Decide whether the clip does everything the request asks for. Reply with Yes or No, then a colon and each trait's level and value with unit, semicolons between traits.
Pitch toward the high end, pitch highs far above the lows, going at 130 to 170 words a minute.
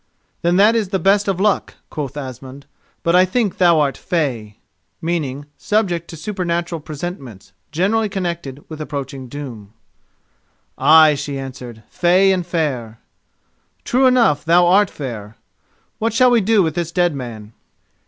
No: medium, 165 Hz; wide, 5.8 semitones; average, 155 wpm